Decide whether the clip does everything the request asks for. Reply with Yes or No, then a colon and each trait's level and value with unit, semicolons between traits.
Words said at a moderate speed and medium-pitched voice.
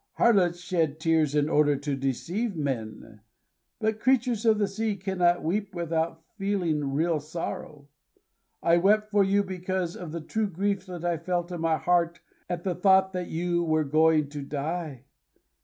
Yes: average, 165 wpm; medium, 175 Hz